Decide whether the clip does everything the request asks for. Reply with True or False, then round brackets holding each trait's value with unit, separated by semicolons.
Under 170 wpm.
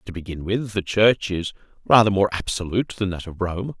False (205 wpm)